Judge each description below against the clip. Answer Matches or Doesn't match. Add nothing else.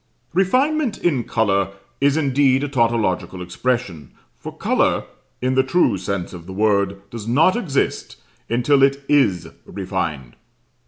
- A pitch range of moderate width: Doesn't match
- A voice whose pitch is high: Doesn't match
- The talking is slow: Matches